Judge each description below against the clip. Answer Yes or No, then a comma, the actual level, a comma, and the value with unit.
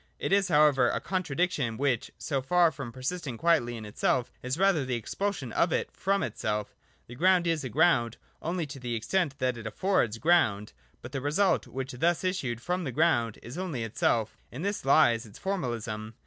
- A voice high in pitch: No, low, 135 Hz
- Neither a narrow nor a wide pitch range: No, wide, 6.7 semitones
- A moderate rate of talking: Yes, average, 190 wpm